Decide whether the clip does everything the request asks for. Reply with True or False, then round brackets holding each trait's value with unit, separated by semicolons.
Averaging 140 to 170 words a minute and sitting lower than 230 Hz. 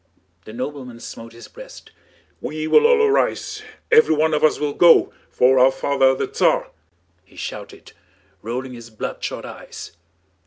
True (145 wpm; 140 Hz)